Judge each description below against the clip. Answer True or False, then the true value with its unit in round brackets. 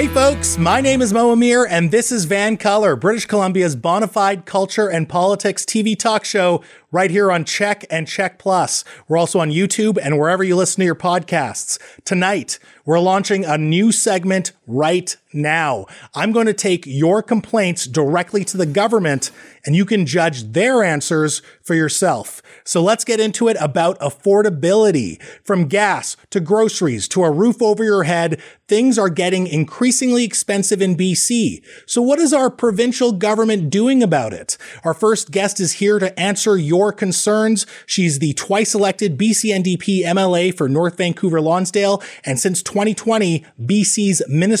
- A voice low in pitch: False (195 Hz)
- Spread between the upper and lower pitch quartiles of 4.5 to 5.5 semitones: False (4.1 semitones)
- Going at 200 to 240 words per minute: False (165 wpm)